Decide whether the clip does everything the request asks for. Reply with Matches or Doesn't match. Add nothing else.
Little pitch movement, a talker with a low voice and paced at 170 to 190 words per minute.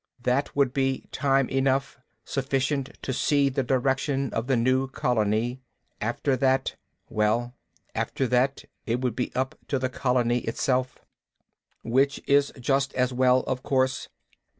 Doesn't match